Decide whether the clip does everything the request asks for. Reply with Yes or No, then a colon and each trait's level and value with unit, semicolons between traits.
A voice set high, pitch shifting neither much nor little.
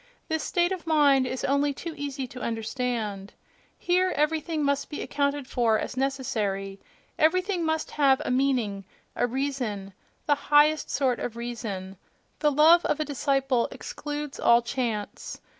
Yes: very high, 270 Hz; average, 4.1 semitones